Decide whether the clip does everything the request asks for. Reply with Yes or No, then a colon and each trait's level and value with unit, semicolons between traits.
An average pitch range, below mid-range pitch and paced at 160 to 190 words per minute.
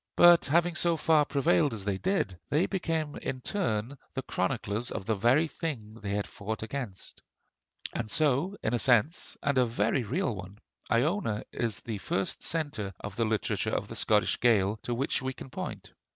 No: wide, 6.5 semitones; low, 125 Hz; average, 180 wpm